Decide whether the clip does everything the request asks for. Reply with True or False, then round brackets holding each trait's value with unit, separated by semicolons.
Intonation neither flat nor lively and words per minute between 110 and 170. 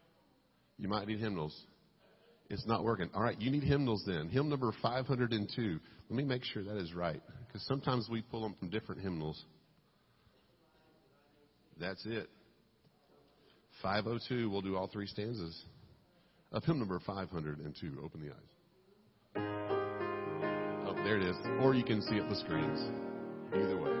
True (4.3 semitones; 150 wpm)